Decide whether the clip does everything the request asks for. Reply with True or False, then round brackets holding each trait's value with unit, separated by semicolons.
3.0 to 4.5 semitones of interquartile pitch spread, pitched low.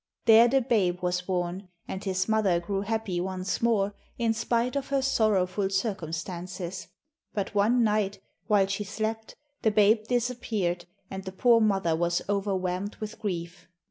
False (3.3 semitones; 200 Hz)